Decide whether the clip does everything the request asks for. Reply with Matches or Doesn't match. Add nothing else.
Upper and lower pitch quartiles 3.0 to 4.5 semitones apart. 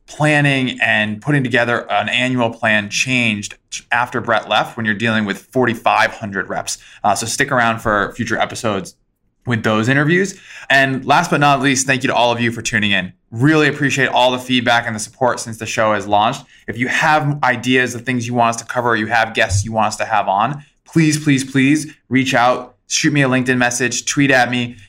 Matches